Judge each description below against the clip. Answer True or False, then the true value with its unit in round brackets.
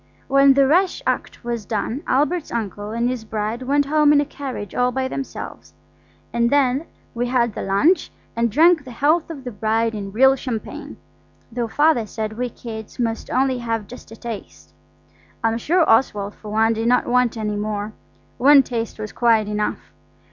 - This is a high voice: True (235 Hz)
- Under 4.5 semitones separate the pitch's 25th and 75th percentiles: True (3.7 semitones)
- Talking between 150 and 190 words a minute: True (180 wpm)